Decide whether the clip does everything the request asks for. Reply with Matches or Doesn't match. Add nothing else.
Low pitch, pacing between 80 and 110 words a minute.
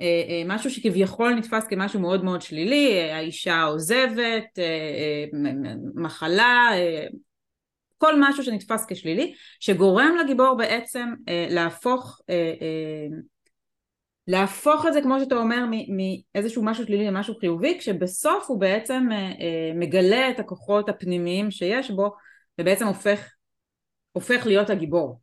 Doesn't match